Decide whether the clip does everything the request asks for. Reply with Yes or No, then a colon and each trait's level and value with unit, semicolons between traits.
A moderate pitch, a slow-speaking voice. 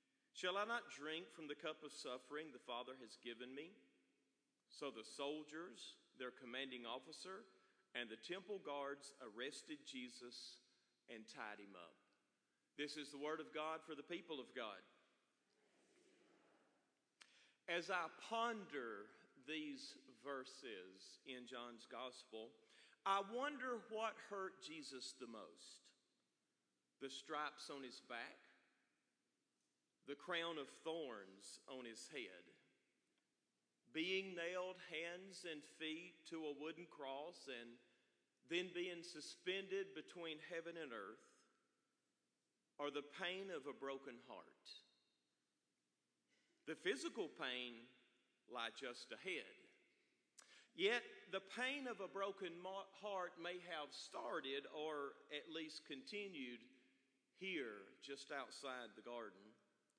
Yes: medium, 155 Hz; slow, 115 wpm